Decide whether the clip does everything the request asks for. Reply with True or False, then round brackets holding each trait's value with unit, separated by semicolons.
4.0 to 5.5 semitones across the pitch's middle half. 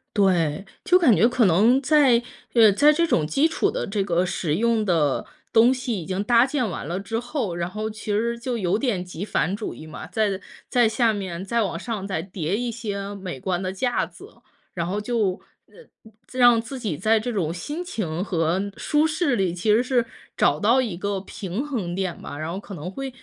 True (5.0 semitones)